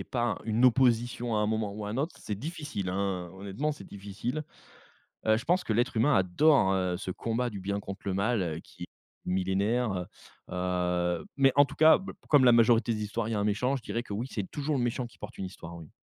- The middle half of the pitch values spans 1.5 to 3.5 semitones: No, average, 4.5 semitones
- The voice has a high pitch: No, low, 110 Hz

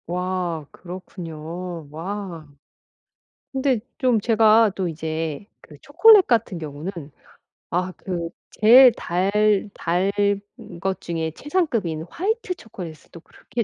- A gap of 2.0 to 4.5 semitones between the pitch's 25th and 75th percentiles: No, average, 5.2 semitones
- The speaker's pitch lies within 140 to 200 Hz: Yes, medium, 185 Hz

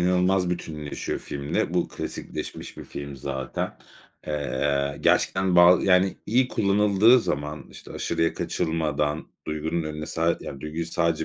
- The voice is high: No, very low, 80 Hz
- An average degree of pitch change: Yes, average, 3.7 semitones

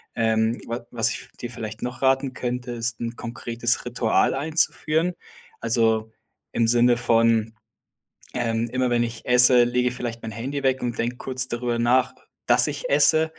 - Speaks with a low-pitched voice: Yes, low, 120 Hz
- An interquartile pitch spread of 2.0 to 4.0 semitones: No, narrow, 1.6 semitones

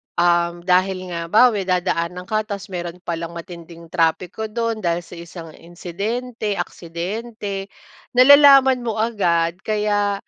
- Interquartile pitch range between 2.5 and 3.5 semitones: No, average, 4.1 semitones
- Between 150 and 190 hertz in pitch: Yes, medium, 185 Hz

